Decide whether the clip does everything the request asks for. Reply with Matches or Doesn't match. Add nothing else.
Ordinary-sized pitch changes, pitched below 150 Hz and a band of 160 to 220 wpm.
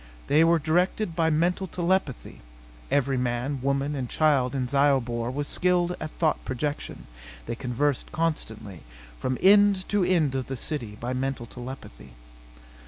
Doesn't match